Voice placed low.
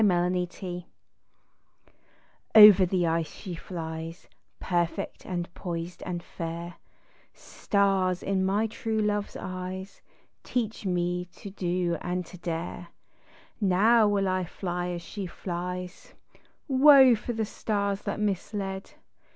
No: medium, 185 Hz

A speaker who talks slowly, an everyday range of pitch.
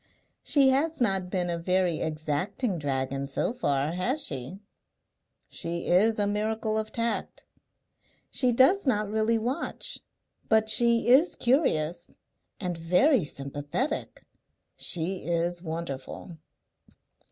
No: slow, 115 wpm; wide, 6.1 semitones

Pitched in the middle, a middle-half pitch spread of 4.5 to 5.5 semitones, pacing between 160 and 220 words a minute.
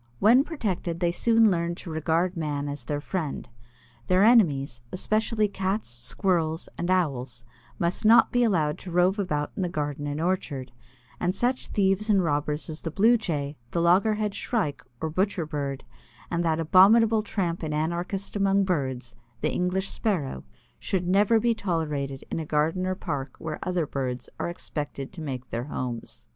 Yes: medium, 170 Hz; average, 4.9 semitones; average, 170 wpm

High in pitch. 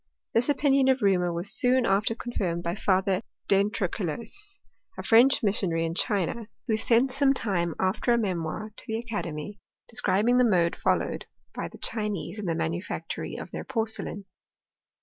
Yes: high, 210 Hz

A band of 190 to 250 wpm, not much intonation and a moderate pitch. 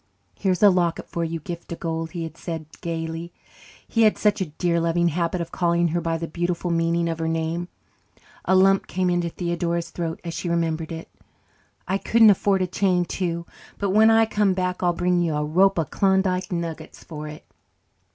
Yes: average, 200 wpm; narrow, 1.9 semitones; medium, 170 Hz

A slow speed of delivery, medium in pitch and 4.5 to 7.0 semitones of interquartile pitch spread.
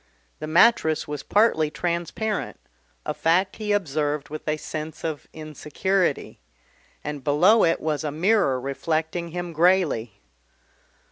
No: slow, 125 wpm; medium, 160 Hz; average, 3.5 semitones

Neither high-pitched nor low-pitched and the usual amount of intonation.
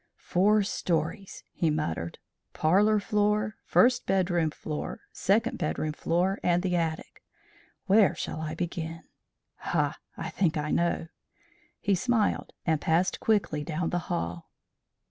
Yes: medium, 175 Hz; average, 4.2 semitones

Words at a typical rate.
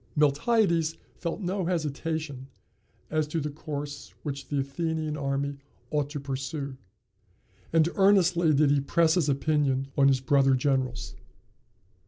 No: slow, 130 wpm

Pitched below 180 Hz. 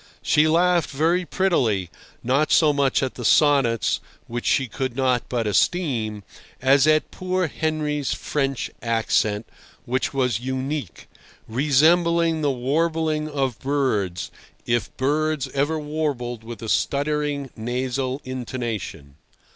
Yes: low, 135 Hz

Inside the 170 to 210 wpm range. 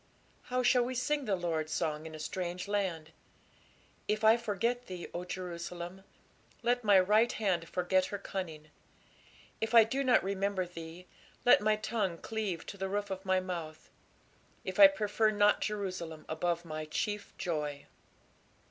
No: average, 155 wpm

